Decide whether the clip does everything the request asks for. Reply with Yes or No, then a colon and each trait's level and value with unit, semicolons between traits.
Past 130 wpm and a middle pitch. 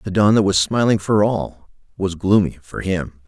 No: average, 200 wpm; very low, 95 Hz